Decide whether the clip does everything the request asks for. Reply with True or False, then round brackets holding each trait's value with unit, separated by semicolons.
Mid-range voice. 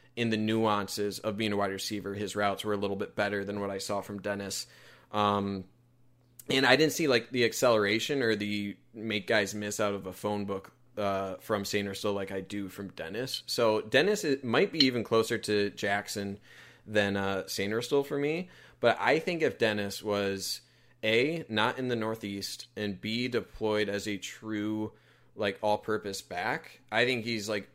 False (105 Hz)